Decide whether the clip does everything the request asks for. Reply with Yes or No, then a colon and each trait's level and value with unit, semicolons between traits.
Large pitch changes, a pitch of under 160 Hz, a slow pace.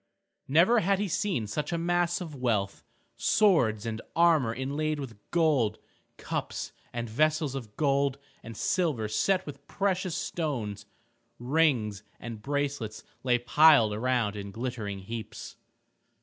Yes: wide, 6.3 semitones; low, 135 Hz; slow, 130 wpm